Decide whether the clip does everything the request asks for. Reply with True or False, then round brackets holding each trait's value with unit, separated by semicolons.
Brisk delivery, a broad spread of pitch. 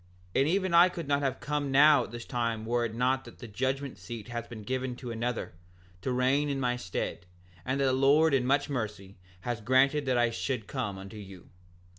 False (215 wpm; 3.1 semitones)